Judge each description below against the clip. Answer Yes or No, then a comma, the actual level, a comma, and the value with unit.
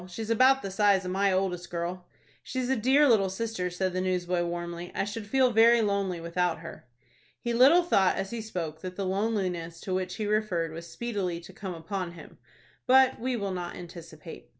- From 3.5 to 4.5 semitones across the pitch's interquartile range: Yes, average, 4.1 semitones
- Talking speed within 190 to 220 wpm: Yes, average, 200 wpm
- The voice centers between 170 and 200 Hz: Yes, high, 190 Hz